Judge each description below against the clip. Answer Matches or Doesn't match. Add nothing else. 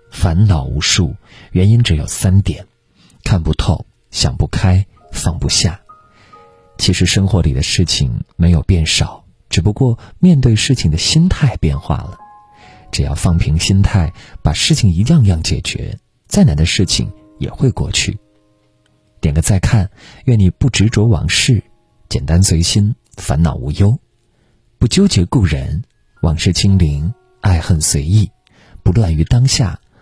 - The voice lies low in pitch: Matches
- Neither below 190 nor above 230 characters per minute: Matches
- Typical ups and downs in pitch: Matches